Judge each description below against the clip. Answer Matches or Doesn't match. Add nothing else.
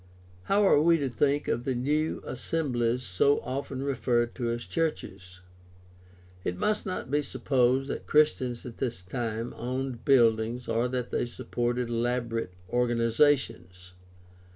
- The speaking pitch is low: Matches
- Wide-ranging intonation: Doesn't match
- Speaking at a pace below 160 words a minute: Matches